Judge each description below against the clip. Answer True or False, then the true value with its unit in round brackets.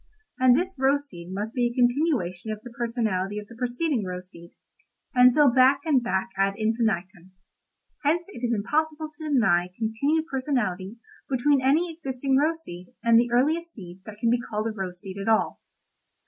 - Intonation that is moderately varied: False (6.0 semitones)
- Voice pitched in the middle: False (240 Hz)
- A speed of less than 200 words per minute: True (175 wpm)